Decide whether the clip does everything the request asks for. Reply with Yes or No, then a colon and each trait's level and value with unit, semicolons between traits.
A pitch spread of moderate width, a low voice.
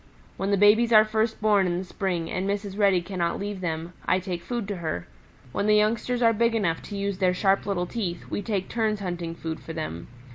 No: average, 3.3 semitones; high, 195 Hz